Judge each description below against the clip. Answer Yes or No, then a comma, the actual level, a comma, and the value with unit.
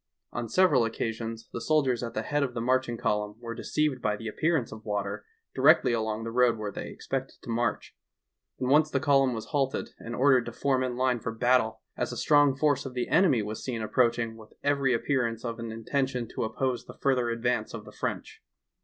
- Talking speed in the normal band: No, fast, 215 wpm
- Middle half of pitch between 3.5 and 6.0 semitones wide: No, average, 2.8 semitones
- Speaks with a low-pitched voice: Yes, low, 120 Hz